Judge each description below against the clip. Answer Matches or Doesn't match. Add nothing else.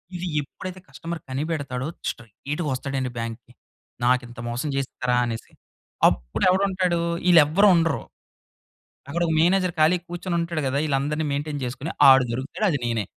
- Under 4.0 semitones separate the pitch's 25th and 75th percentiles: Doesn't match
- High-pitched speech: Doesn't match